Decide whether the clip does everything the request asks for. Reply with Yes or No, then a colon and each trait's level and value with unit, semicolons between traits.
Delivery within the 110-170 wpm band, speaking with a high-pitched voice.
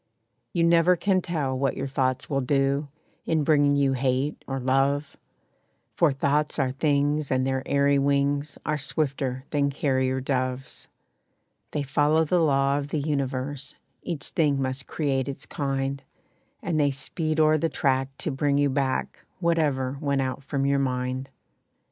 No: average, 155 wpm; medium, 140 Hz